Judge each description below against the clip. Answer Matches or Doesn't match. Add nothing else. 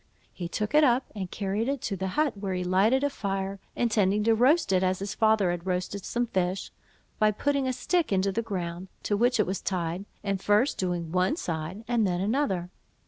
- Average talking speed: Doesn't match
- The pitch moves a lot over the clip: Doesn't match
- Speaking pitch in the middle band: Doesn't match